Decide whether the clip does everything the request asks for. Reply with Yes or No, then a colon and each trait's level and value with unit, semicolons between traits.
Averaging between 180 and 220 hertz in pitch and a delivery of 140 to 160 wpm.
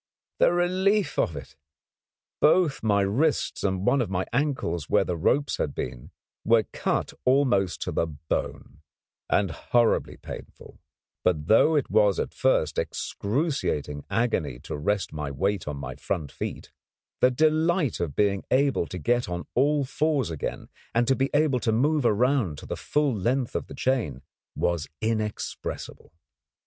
No: low, 110 Hz; average, 155 wpm